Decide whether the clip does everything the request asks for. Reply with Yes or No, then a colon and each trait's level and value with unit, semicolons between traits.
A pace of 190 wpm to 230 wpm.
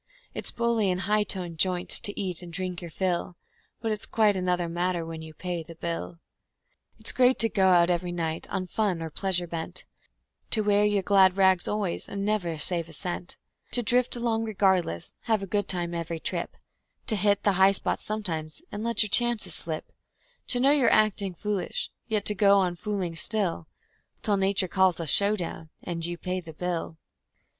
Yes: average, 200 wpm